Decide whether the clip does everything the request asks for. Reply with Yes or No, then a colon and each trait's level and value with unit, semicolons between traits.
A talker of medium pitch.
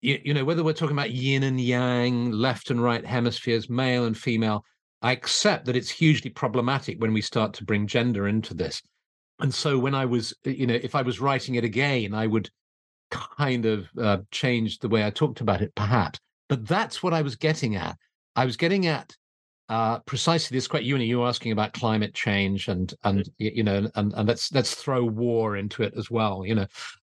No: low, 120 Hz